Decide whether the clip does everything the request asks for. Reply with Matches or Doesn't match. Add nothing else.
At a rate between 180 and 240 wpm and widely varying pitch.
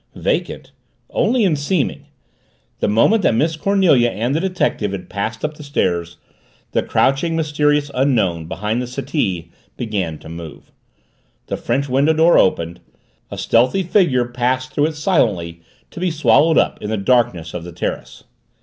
Doesn't match